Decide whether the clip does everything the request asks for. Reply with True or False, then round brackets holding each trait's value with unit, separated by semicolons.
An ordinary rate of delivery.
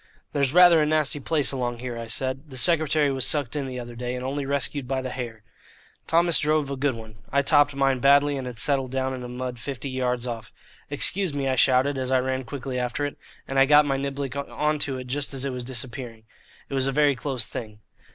False (235 wpm)